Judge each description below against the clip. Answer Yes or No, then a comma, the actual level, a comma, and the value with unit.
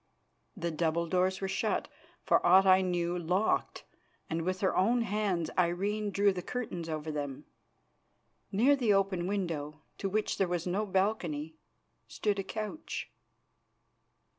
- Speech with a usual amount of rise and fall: Yes, average, 3.1 semitones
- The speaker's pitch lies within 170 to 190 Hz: Yes, medium, 185 Hz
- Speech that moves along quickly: No, average, 140 wpm